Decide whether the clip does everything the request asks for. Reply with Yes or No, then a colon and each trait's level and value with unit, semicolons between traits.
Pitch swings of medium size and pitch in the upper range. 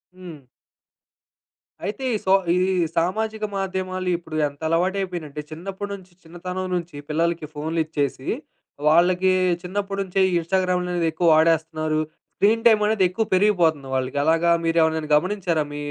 No: average, 3.0 semitones; medium, 175 Hz